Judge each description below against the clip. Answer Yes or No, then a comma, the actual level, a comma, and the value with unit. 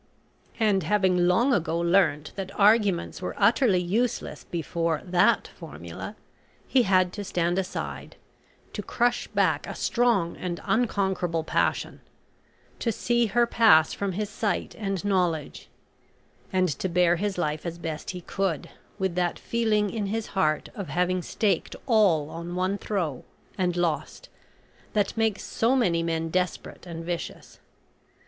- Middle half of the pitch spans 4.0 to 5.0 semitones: No, average, 3.6 semitones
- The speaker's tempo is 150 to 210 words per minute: No, average, 140 wpm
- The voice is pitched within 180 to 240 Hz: Yes, medium, 185 Hz